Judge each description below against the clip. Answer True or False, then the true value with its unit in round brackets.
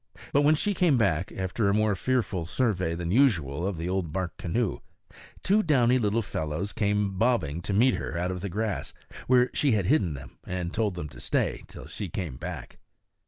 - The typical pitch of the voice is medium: False (100 Hz)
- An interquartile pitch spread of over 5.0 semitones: True (5.6 semitones)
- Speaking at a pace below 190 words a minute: False (200 wpm)